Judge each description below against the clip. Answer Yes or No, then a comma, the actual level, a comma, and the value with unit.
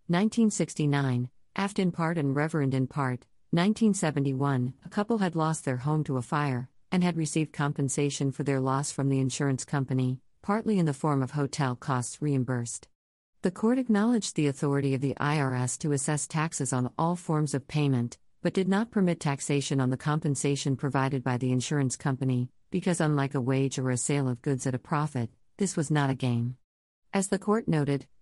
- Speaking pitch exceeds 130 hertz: Yes, medium, 140 Hz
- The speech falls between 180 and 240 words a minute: Yes, average, 185 wpm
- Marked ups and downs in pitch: No, average, 3.6 semitones